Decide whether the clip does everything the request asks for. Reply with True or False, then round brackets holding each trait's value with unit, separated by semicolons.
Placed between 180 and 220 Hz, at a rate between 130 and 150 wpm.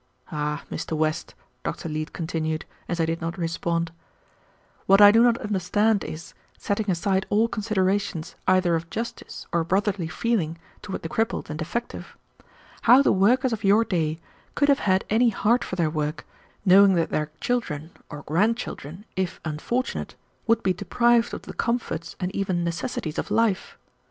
False (185 Hz; 165 wpm)